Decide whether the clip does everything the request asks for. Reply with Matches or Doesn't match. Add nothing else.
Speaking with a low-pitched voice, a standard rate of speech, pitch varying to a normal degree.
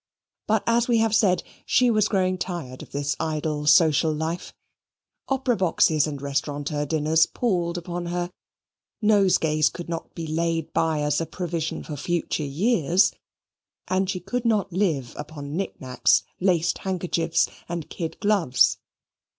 Doesn't match